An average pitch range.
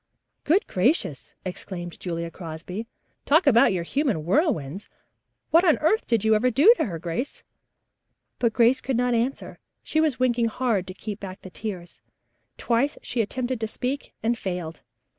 No: wide, 6.1 semitones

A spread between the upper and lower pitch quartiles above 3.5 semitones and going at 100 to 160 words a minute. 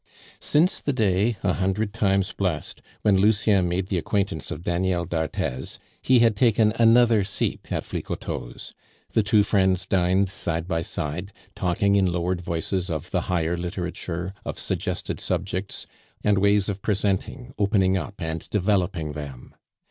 No: average, 2.9 semitones; average, 150 wpm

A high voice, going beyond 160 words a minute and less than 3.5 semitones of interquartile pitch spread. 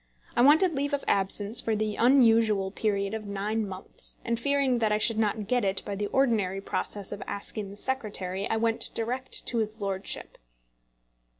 Yes: high, 215 Hz; average, 180 wpm; average, 2.9 semitones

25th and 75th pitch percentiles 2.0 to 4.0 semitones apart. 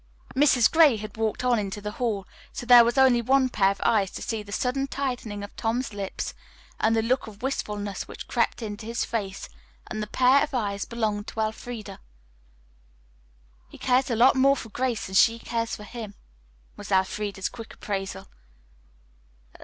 Yes: average, 3.3 semitones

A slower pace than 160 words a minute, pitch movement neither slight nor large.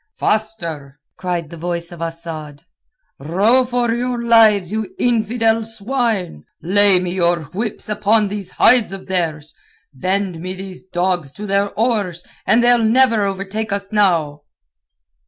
Yes: average, 140 wpm; average, 4.3 semitones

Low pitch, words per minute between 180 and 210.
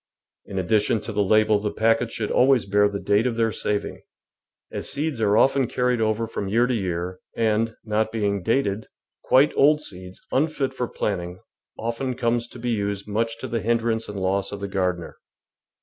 Yes: low, 110 Hz; average, 185 wpm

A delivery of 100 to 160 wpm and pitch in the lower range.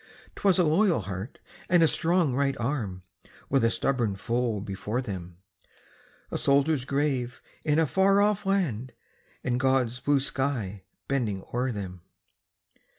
Yes: average, 140 wpm; low, 130 Hz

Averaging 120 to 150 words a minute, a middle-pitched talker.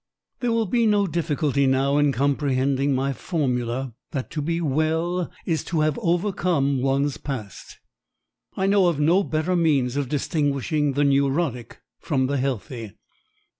Yes: average, 145 wpm; medium, 145 Hz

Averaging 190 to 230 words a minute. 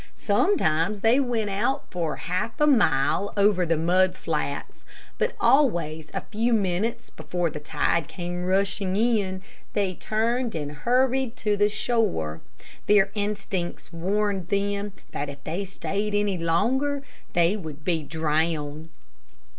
No: slow, 135 wpm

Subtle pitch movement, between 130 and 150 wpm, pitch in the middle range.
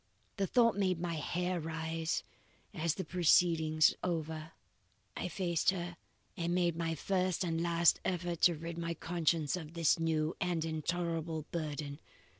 Yes: narrow, 1.7 semitones; average, 145 wpm; medium, 170 Hz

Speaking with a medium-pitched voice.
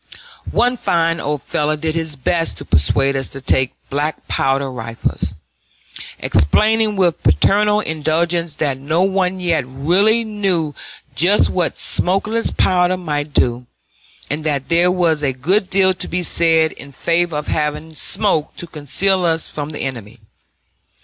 Yes: medium, 160 Hz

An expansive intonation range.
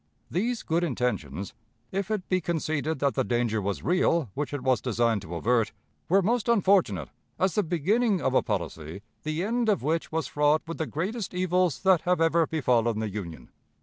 Yes: wide, 7.7 semitones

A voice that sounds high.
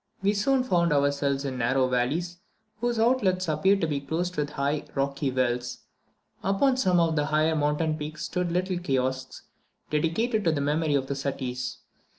No: medium, 155 Hz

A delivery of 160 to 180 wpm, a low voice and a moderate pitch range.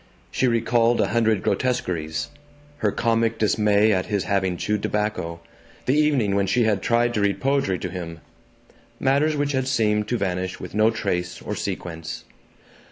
Yes: average, 165 wpm; low, 105 Hz; average, 4.0 semitones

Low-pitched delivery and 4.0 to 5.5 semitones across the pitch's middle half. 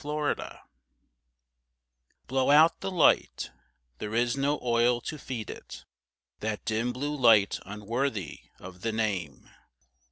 Yes: low, 120 Hz; average, 4.8 semitones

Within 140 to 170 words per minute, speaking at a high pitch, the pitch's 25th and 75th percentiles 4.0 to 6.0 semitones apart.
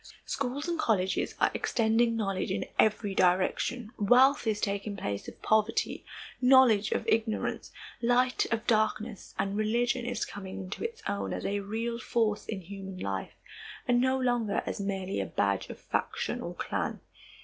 No: average, 160 wpm; high, 215 Hz; average, 3.6 semitones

